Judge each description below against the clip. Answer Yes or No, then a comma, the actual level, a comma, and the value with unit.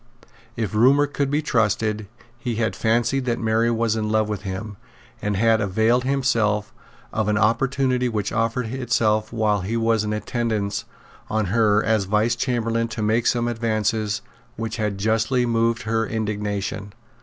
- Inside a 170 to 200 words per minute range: No, average, 155 wpm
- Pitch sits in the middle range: No, low, 110 Hz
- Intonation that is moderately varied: No, narrow, 1.7 semitones